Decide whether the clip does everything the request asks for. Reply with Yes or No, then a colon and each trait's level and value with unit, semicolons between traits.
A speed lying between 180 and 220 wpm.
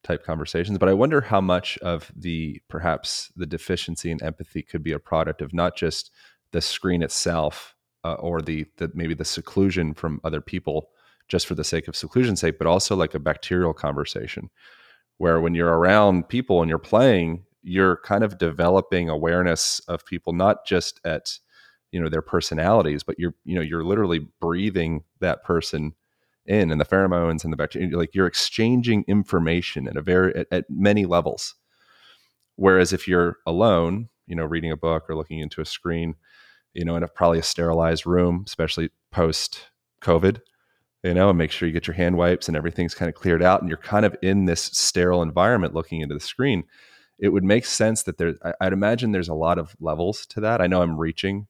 Yes: average, 195 wpm